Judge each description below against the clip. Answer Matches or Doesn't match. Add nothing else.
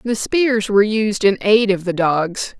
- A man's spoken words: Doesn't match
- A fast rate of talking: Matches